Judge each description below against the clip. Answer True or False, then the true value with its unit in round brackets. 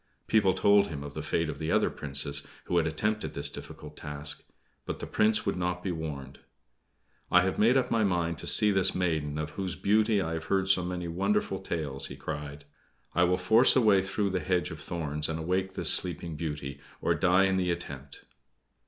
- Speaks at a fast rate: True (210 wpm)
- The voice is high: False (90 Hz)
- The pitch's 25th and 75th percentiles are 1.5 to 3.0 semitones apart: False (3.9 semitones)